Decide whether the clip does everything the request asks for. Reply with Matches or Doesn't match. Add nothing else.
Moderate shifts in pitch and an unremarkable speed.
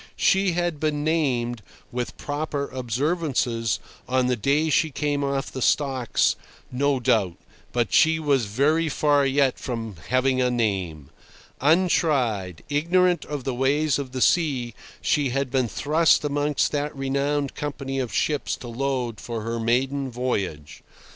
Matches